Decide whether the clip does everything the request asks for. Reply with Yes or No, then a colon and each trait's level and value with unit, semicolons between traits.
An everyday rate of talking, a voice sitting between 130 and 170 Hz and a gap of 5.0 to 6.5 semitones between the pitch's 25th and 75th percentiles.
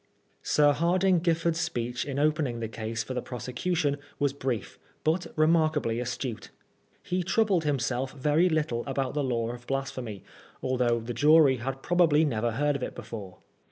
No: average, 160 wpm; low, 135 Hz; average, 4.5 semitones